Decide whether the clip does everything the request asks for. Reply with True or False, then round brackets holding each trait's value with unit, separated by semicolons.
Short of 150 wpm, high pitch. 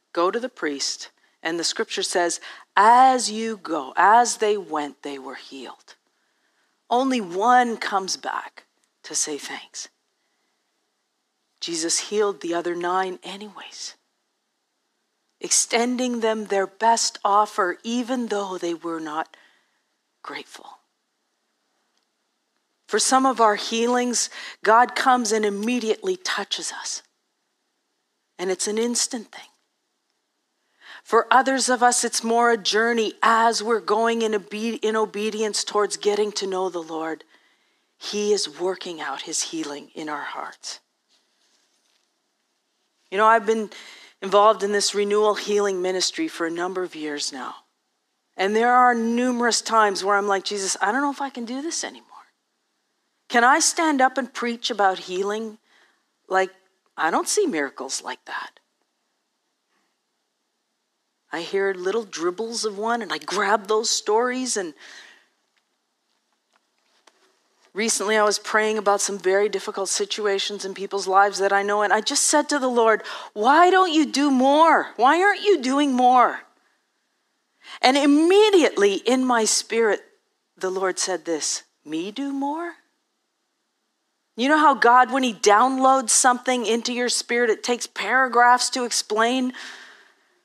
True (140 wpm; 225 Hz)